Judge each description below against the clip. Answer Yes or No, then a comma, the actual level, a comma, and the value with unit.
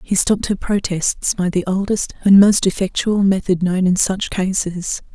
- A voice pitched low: No, high, 190 Hz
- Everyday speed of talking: Yes, average, 175 wpm